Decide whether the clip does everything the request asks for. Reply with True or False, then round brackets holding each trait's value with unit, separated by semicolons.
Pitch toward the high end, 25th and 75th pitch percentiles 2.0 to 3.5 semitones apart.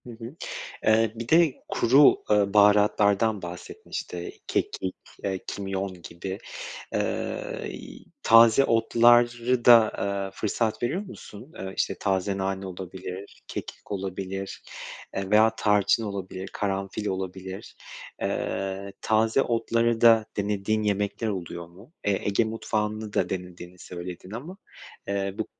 False (100 Hz; 2.9 semitones)